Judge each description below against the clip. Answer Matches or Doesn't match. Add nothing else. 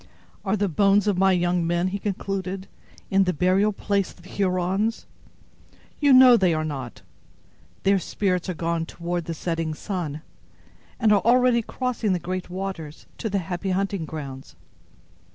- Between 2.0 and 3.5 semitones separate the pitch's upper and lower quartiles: Matches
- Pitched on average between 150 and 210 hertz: Matches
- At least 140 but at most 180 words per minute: Matches